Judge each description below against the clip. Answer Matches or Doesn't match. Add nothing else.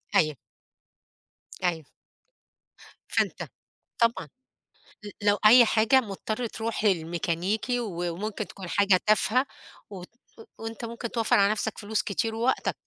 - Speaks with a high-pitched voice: Matches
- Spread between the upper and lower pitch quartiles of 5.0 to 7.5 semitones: Doesn't match